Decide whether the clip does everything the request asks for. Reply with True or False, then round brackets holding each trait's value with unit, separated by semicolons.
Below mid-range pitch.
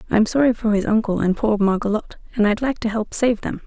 False (220 Hz)